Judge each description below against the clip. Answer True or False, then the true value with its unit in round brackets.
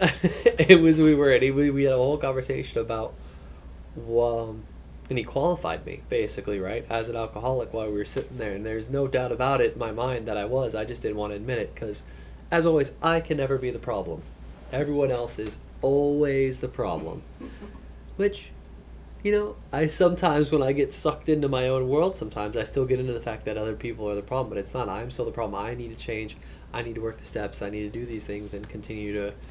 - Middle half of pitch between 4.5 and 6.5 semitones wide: True (5.1 semitones)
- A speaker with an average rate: False (230 wpm)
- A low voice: True (120 Hz)